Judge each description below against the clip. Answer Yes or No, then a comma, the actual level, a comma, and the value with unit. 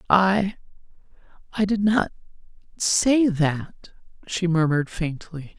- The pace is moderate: No, slow, 75 wpm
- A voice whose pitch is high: No, medium, 180 Hz